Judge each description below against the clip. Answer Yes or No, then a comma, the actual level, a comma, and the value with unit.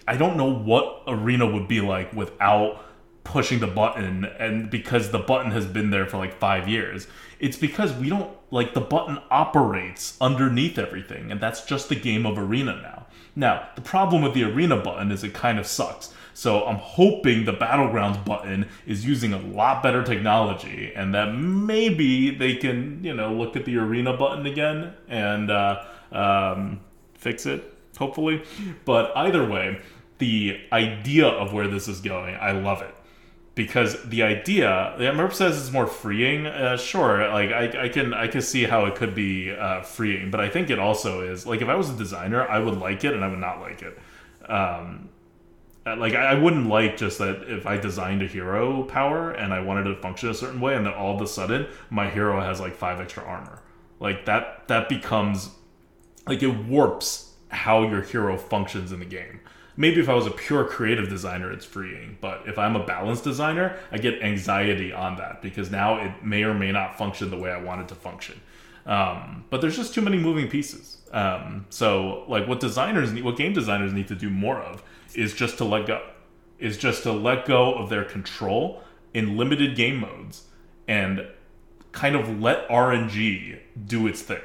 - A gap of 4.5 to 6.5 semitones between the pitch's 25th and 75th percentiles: Yes, average, 4.8 semitones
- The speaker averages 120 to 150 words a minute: No, average, 195 wpm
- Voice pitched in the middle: No, low, 110 Hz